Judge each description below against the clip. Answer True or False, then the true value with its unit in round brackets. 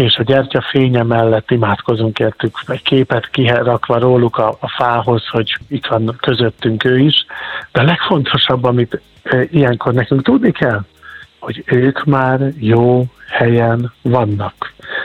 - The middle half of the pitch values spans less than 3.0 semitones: True (2.5 semitones)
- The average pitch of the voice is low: True (125 Hz)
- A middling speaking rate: True (130 wpm)